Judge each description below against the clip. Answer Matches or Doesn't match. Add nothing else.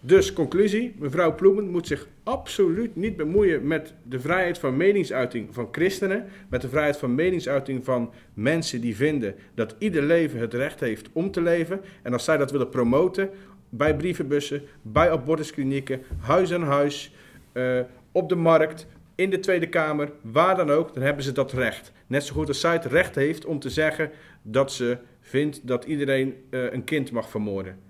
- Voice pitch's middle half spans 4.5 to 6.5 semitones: Matches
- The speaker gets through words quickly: Doesn't match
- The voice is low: Doesn't match